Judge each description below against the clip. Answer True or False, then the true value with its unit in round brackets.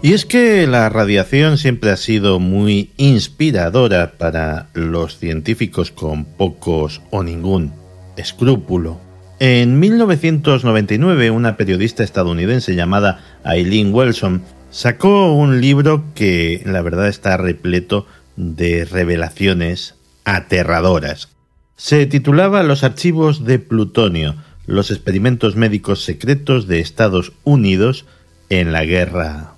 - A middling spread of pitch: False (6.6 semitones)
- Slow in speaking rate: True (110 wpm)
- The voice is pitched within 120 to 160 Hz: False (95 Hz)